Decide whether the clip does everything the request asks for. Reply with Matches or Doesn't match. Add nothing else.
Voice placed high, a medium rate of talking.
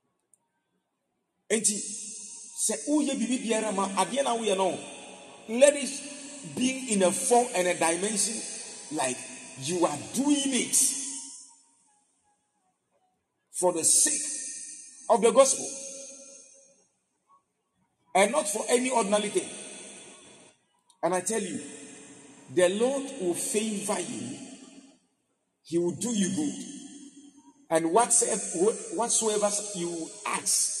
Doesn't match